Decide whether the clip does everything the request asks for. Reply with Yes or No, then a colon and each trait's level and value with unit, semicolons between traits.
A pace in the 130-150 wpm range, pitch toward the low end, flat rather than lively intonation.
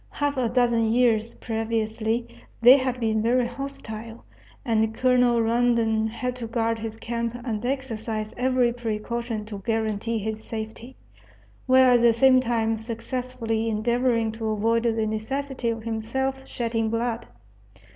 No: slow, 135 wpm; high, 230 Hz; narrow, 1.8 semitones